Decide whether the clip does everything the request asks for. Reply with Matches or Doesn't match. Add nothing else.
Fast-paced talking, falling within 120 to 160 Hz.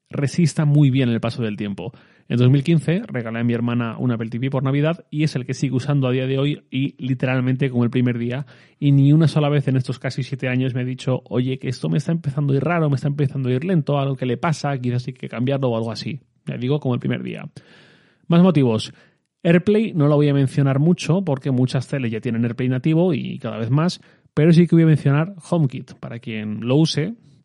Matches